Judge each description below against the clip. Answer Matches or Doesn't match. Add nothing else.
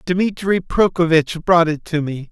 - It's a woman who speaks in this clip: Doesn't match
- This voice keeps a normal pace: Matches